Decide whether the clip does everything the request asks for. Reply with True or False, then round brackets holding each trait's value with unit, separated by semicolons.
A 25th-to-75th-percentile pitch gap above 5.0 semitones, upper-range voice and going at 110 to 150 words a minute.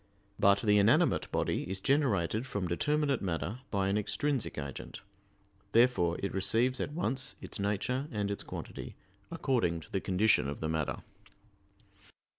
False (5.4 semitones; 100 Hz; 145 wpm)